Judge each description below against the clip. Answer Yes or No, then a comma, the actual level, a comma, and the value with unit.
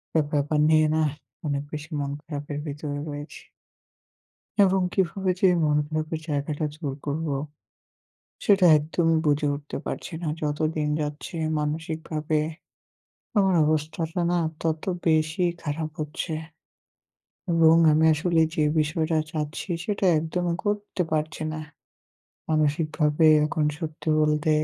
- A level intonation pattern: Yes, narrow, 1.6 semitones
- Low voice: No, medium, 155 Hz